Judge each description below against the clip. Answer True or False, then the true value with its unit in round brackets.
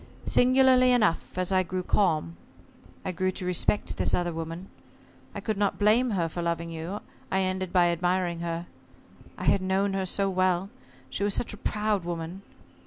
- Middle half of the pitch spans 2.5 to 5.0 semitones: True (2.8 semitones)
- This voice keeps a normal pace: True (175 wpm)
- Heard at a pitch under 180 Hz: False (185 Hz)